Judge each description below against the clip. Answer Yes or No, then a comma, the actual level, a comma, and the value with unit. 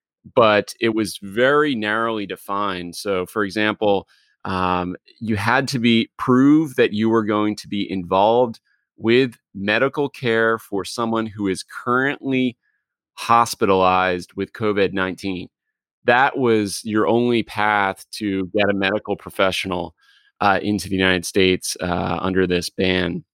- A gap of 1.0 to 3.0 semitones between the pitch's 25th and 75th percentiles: No, average, 3.4 semitones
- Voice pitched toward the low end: Yes, low, 100 Hz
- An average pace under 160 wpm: Yes, slow, 135 wpm